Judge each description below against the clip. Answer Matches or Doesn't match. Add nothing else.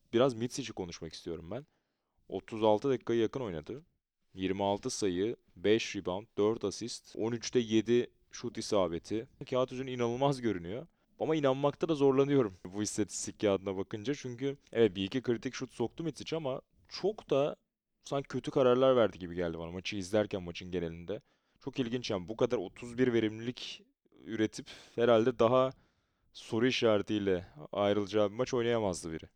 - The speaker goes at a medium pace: Doesn't match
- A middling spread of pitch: Matches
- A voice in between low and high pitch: Doesn't match